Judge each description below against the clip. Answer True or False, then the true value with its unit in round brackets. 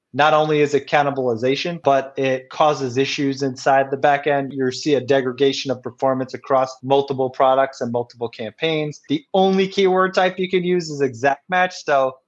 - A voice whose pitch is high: False (140 Hz)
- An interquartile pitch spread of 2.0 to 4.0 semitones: True (2.6 semitones)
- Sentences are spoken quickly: False (170 wpm)